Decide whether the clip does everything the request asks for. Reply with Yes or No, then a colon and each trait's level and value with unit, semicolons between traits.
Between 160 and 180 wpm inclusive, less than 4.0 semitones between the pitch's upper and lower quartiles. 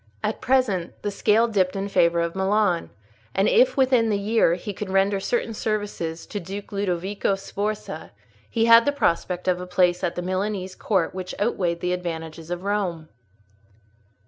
Yes: average, 170 wpm; average, 3.0 semitones